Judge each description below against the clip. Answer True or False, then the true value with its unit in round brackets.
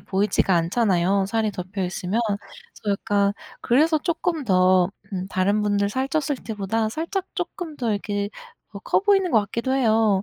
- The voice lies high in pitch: True (210 Hz)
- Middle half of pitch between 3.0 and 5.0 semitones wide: False (5.5 semitones)